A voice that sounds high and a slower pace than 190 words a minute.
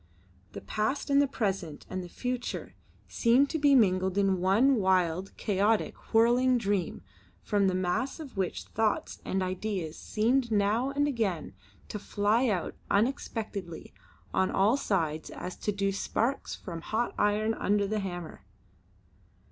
Yes: high, 205 Hz; average, 140 wpm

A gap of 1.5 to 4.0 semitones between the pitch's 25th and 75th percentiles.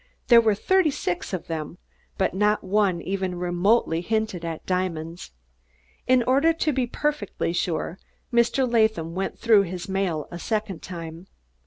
No: average, 4.7 semitones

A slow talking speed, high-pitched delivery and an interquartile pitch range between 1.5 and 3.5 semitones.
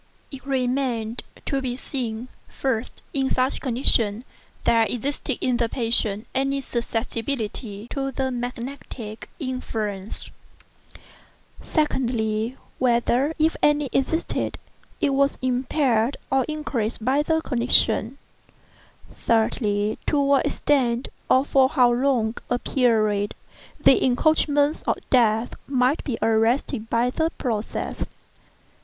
Yes: slow, 110 wpm; very high, 250 Hz; average, 3.2 semitones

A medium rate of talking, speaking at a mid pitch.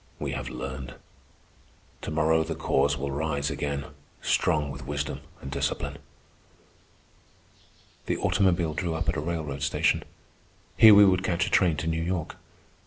No: average, 150 wpm; very low, 80 Hz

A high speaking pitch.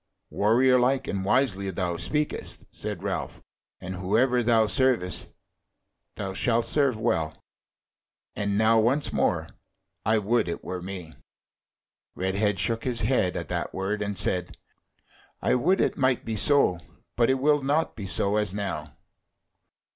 No: low, 110 Hz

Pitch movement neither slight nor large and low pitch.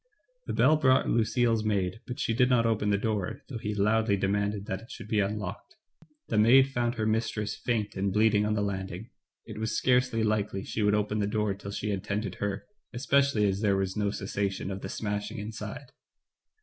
No: narrow, 2.1 semitones; low, 105 Hz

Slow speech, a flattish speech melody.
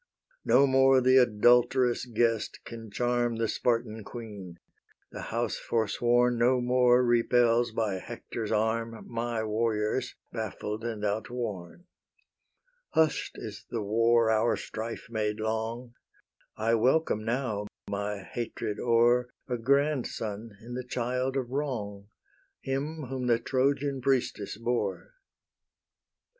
Yes: slow, 115 wpm; narrow, 2.3 semitones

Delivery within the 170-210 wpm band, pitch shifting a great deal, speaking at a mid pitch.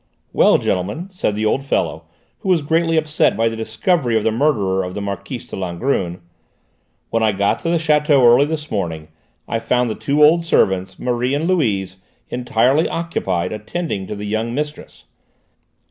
No: average, 175 wpm; wide, 7.0 semitones; low, 120 Hz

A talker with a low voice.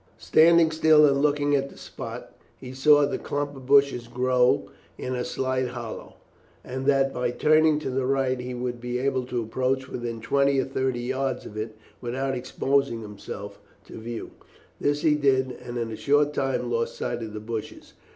Yes: low, 130 Hz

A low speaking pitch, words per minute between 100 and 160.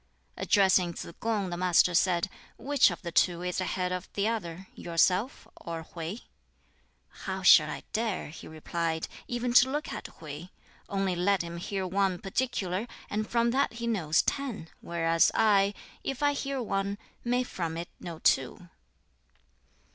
No: high, 190 Hz; average, 155 wpm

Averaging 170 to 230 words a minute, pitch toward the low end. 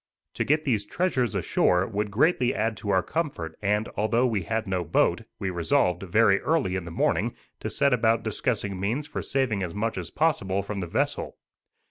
Yes: average, 190 wpm; low, 105 Hz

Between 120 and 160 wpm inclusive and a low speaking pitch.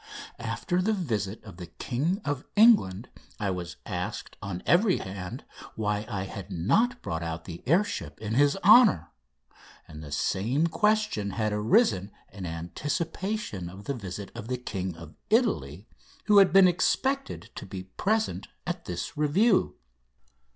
Yes: average, 150 wpm; low, 110 Hz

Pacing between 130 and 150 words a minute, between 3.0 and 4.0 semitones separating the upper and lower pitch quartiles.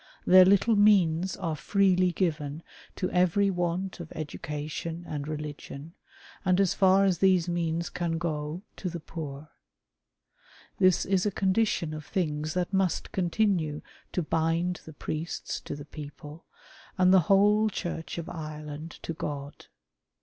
Yes: average, 140 wpm; average, 3.4 semitones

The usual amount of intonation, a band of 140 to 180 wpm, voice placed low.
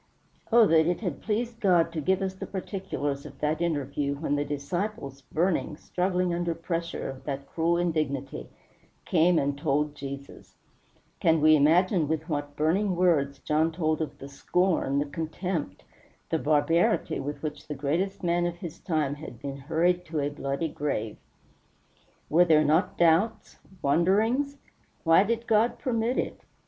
No: average, 3.7 semitones; average, 155 wpm; medium, 160 Hz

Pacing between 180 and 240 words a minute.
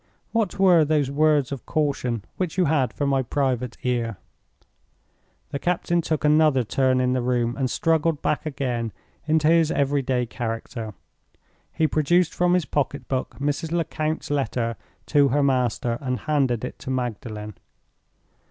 No: average, 150 wpm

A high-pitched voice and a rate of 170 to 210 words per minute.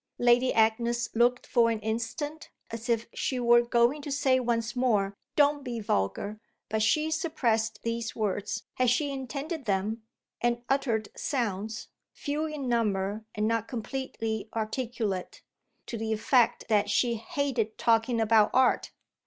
No: high, 235 Hz; average, 145 wpm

